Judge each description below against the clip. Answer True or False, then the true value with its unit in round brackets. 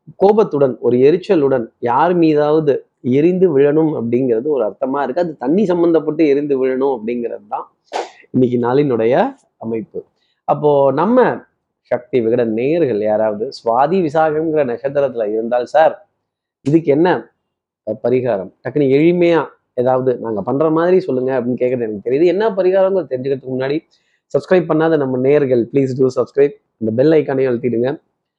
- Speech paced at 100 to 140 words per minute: True (130 wpm)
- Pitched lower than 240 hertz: True (140 Hz)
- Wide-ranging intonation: False (4.4 semitones)